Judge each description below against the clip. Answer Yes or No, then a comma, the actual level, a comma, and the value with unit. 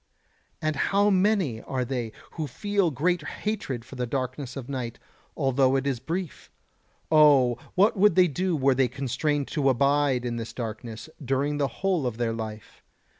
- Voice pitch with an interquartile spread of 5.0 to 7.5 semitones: No, average, 4.4 semitones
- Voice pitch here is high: No, low, 135 Hz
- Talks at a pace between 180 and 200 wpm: No, average, 170 wpm